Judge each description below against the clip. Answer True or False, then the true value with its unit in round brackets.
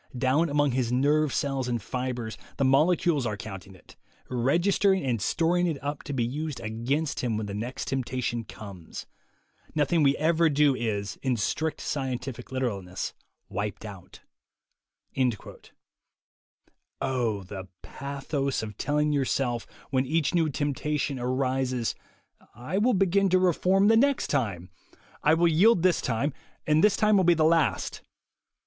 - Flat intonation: False (4.9 semitones)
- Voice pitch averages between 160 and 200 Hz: False (135 Hz)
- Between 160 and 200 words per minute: False (140 wpm)